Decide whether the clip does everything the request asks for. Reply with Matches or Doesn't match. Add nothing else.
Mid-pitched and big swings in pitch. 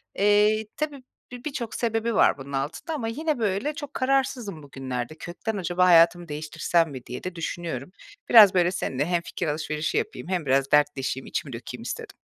Matches